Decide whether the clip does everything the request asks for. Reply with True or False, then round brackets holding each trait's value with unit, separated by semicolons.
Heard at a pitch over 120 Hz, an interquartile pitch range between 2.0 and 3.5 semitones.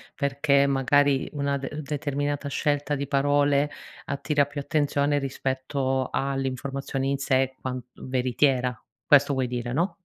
False (140 Hz; 1.4 semitones)